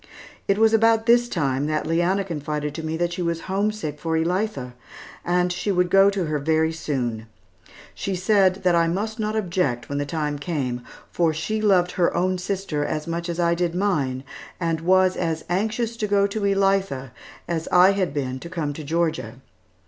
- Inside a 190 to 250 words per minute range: Yes, average, 195 wpm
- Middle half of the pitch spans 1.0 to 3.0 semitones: No, average, 4.2 semitones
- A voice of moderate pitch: Yes, medium, 175 Hz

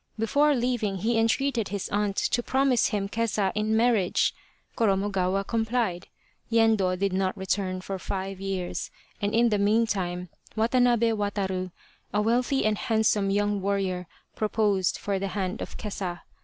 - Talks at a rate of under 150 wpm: Yes, average, 140 wpm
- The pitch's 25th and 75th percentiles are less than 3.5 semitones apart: Yes, average, 2.9 semitones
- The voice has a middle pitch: No, high, 205 Hz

